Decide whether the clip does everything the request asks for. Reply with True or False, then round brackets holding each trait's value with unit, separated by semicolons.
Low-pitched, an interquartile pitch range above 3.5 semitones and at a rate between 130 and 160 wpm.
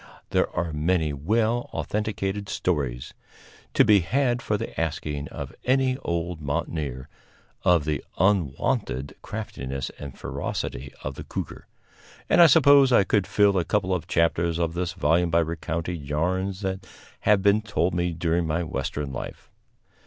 True (85 Hz; 5.0 semitones; 150 wpm)